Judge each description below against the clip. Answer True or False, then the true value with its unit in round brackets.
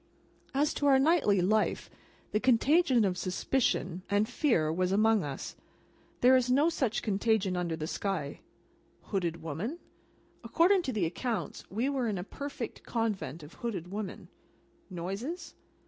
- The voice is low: False (215 Hz)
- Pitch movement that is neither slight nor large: False (6.3 semitones)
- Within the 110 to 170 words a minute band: True (145 wpm)